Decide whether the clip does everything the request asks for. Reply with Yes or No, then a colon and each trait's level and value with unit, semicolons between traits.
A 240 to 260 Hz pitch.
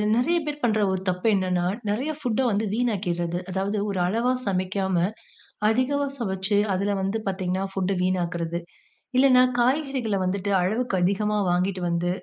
No: high, 195 Hz